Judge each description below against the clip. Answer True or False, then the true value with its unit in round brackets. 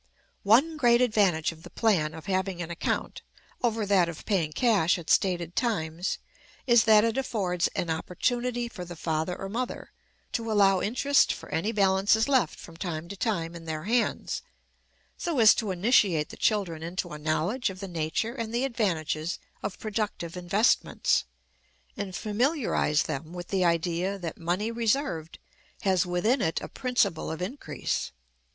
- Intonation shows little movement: False (5.1 semitones)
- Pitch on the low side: False (195 Hz)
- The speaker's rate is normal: True (160 wpm)